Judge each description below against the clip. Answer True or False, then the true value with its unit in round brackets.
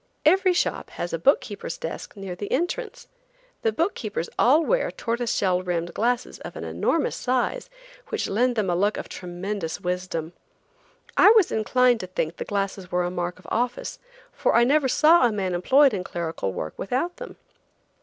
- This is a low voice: False (210 Hz)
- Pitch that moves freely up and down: True (6.8 semitones)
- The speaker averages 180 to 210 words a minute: True (185 wpm)